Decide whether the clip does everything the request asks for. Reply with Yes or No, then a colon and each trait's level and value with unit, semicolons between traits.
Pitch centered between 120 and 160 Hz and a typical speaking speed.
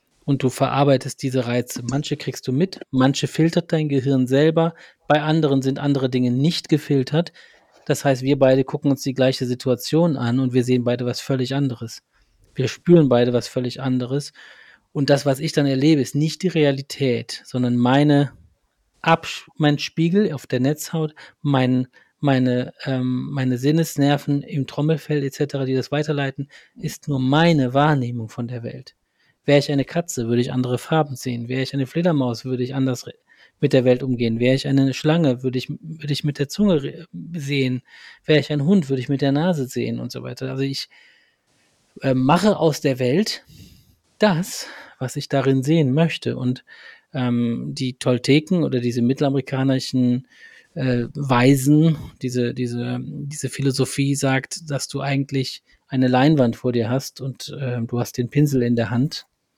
Yes: low, 135 Hz; average, 170 wpm